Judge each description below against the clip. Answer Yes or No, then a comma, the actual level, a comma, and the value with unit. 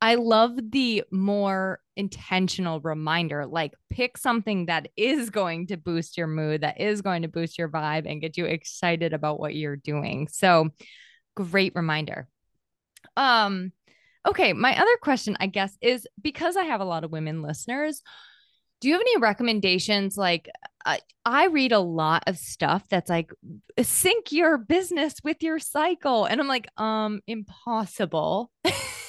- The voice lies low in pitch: No, high, 195 Hz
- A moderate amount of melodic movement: No, wide, 7.2 semitones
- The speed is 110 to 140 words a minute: No, average, 155 wpm